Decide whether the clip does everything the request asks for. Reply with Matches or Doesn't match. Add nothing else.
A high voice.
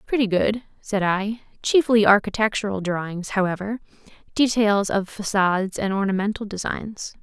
Matches